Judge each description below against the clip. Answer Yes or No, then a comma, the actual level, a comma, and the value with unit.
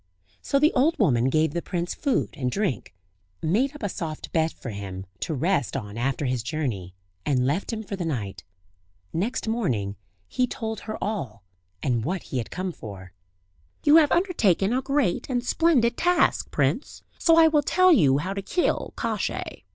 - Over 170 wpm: Yes, average, 180 wpm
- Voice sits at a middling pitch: Yes, medium, 180 Hz